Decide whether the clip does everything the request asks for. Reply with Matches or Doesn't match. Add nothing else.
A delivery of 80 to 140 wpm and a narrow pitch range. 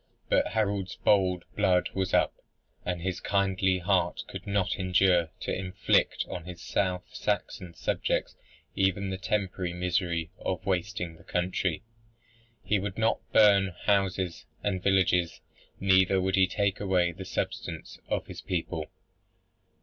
Matches